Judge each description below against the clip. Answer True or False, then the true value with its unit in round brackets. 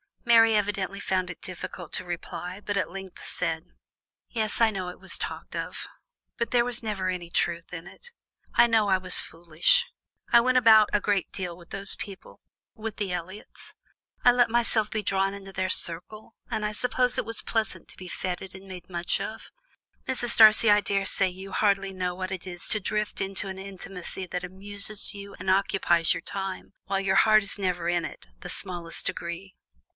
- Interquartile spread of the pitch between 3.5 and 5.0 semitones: False (2.8 semitones)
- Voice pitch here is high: True (195 Hz)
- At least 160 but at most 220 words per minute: True (190 wpm)